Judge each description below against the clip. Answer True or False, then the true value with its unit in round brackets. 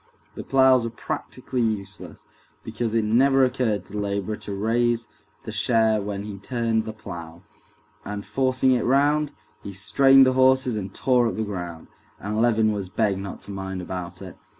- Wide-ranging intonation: False (4.1 semitones)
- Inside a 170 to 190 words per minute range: True (175 wpm)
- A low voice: True (110 Hz)